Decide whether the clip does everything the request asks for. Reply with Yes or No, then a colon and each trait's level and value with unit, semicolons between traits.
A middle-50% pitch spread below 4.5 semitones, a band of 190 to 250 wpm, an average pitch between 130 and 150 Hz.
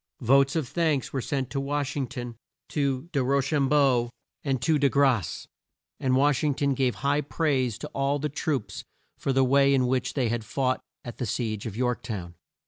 Yes: narrow, 2.4 semitones; average, 200 wpm; low, 135 Hz